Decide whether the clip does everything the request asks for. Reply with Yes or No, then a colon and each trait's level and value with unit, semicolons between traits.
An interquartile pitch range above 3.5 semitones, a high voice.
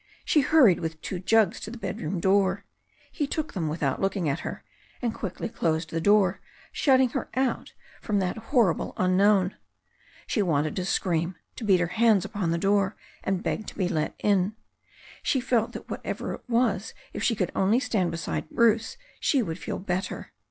Yes: average, 4.2 semitones; high, 195 Hz